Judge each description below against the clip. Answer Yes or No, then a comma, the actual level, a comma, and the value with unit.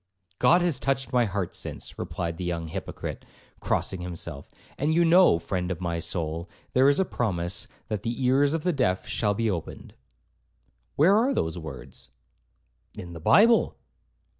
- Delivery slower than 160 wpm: No, average, 165 wpm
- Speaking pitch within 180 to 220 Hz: No, low, 100 Hz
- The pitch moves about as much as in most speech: No, wide, 8.7 semitones